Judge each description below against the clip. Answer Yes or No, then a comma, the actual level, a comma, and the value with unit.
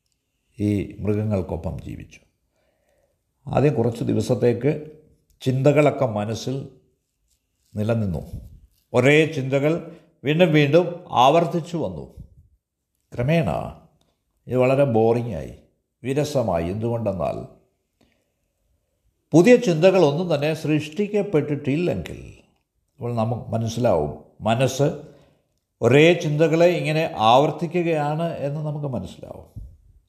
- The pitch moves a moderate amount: No, wide, 6.7 semitones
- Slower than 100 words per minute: Yes, average, 70 wpm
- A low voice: Yes, low, 130 Hz